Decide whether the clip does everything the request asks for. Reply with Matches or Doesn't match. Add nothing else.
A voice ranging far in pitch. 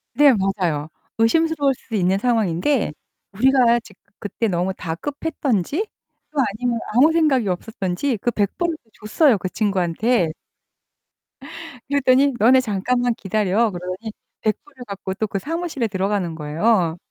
Matches